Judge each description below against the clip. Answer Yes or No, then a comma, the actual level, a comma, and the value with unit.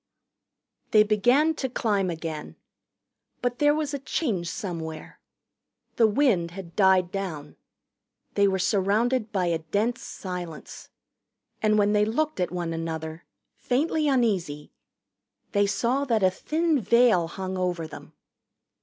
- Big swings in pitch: Yes, wide, 5.8 semitones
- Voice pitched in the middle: No, high, 200 Hz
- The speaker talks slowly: Yes, slow, 130 wpm